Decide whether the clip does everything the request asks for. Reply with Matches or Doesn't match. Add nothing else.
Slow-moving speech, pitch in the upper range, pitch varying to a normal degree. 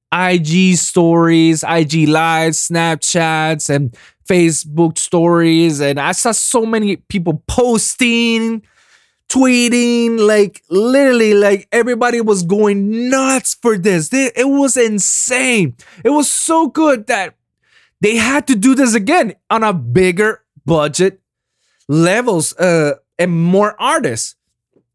Doesn't match